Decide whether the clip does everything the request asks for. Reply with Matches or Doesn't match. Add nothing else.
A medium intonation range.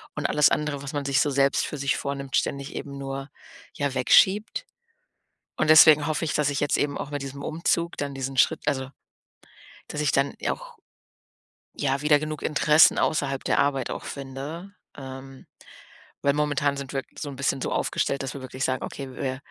Doesn't match